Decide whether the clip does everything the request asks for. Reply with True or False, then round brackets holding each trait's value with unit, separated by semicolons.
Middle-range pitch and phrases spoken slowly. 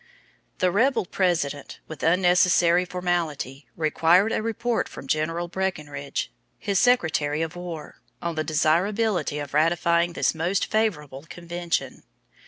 True (170 Hz; 120 wpm)